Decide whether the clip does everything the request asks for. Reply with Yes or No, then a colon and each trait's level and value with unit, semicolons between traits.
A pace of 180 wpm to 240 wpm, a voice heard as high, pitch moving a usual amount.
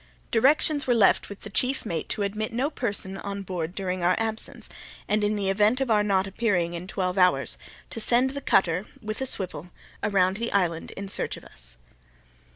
Yes: average, 195 wpm; high, 200 Hz; average, 3.5 semitones